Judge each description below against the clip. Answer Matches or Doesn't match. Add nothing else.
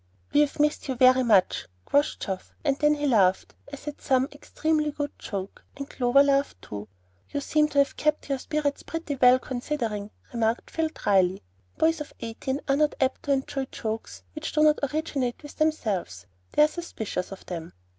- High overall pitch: Matches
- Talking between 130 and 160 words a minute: Doesn't match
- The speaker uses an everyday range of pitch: Matches